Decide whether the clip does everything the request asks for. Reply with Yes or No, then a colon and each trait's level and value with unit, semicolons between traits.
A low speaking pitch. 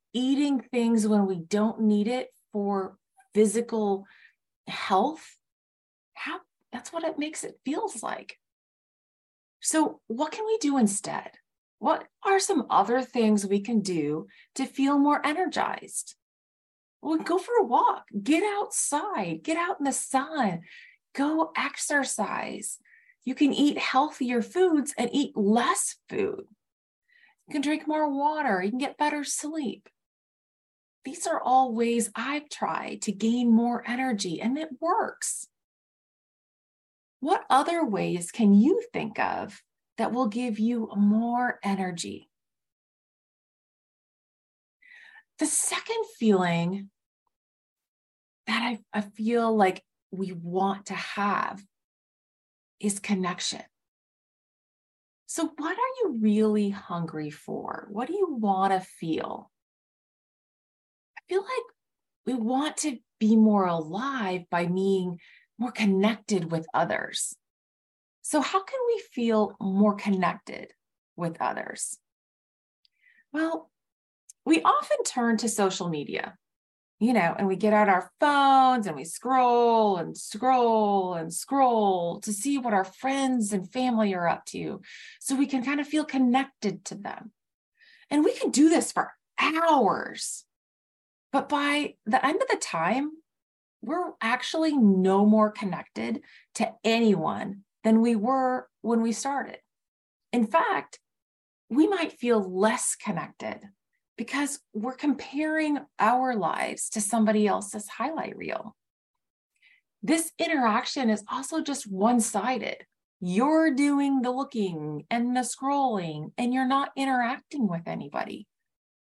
No: high, 245 Hz